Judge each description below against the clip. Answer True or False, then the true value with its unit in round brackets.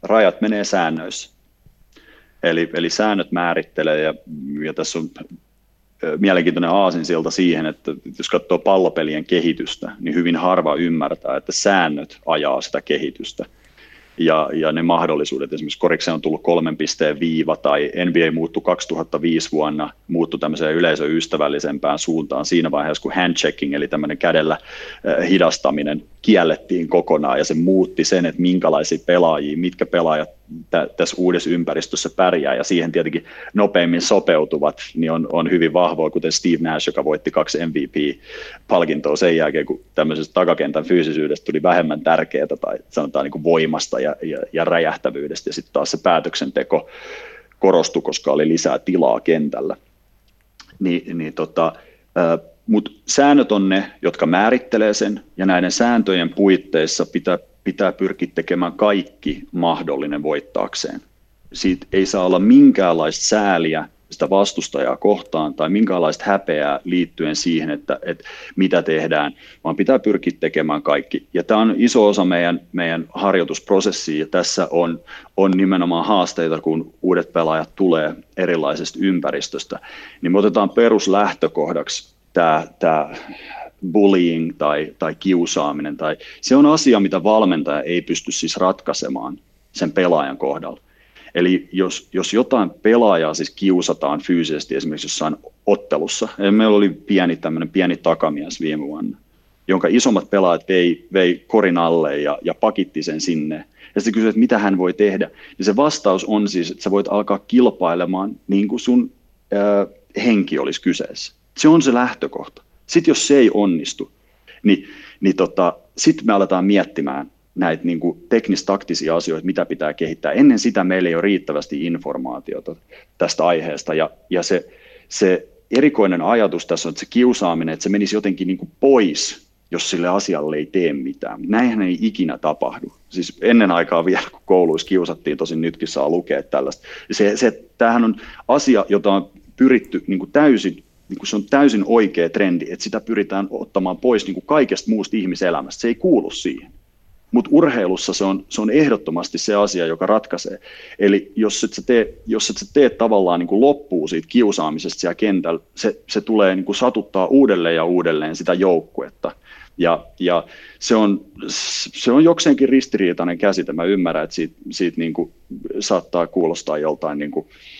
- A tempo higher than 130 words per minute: True (150 wpm)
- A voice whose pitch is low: True (90 Hz)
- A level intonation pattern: False (3.8 semitones)